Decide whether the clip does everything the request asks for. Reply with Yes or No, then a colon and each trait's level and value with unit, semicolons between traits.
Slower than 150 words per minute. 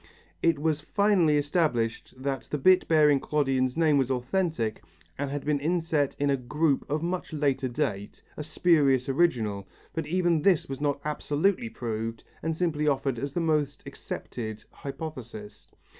No: average, 155 wpm